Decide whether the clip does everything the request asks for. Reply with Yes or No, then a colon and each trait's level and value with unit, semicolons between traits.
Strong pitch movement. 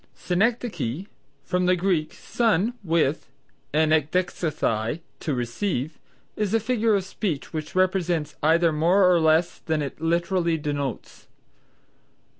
No: average, 3.5 semitones